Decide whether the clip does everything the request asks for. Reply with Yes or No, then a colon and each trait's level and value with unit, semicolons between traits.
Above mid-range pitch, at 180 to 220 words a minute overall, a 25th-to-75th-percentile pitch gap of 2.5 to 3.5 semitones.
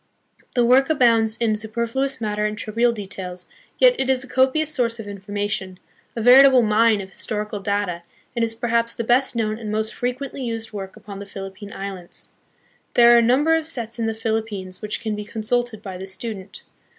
Yes: high, 225 Hz; average, 200 wpm; average, 2.9 semitones